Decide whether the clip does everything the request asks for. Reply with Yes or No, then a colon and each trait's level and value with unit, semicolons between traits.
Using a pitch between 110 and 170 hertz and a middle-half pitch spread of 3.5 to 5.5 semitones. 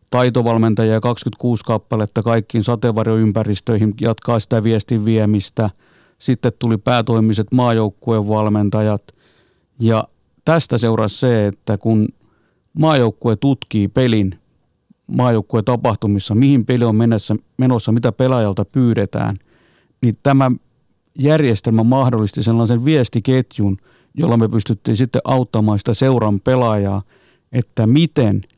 No: low, 115 Hz; narrow, 2.5 semitones